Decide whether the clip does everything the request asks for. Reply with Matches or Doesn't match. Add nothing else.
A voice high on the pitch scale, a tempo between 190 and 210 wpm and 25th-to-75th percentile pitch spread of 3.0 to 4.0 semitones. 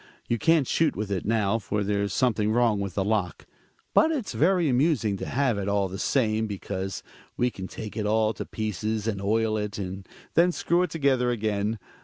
Doesn't match